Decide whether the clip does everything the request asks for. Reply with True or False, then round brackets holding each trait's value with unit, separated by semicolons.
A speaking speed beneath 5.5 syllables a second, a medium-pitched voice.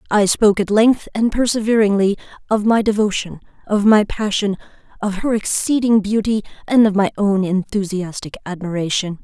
False (5.2 syllables/s; 205 Hz)